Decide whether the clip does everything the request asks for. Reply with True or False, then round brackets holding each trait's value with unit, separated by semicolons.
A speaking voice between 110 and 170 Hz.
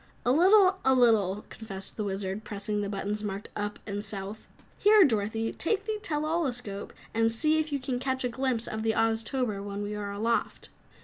False (225 Hz)